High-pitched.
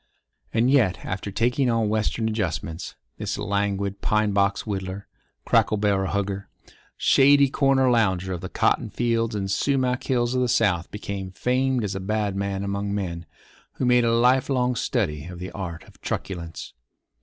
No: low, 105 Hz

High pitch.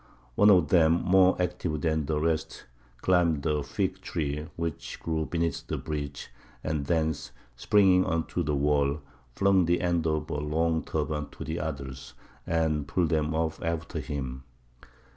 No: very low, 80 Hz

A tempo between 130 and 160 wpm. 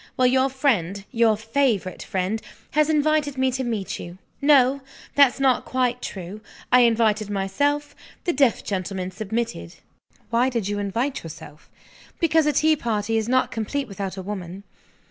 Yes: average, 155 wpm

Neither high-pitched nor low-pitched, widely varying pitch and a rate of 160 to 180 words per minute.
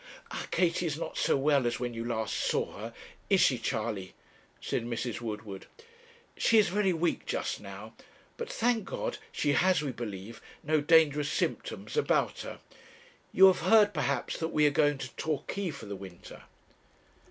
Yes: medium, 145 Hz; wide, 7.1 semitones; average, 170 wpm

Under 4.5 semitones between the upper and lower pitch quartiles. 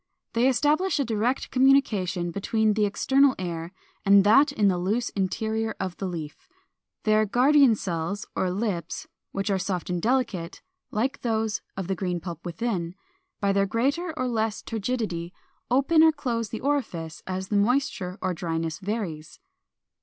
No: average, 5.3 semitones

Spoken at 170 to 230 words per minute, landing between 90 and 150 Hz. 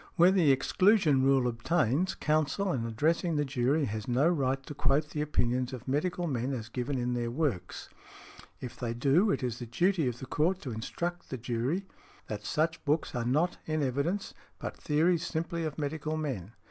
Yes: average, 185 wpm; medium, 140 Hz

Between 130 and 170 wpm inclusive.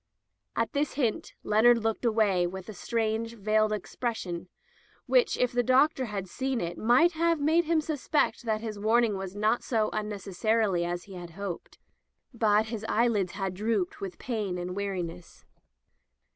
Yes: average, 160 wpm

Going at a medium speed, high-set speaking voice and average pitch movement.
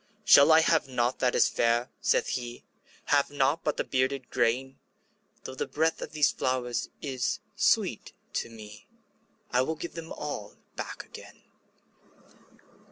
No: average, 150 wpm; low, 130 Hz; average, 3.4 semitones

